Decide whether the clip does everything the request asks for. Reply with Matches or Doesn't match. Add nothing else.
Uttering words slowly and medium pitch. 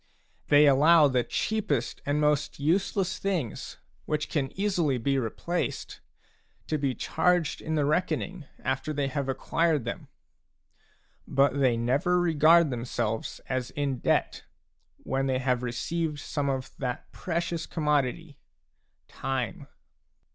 Matches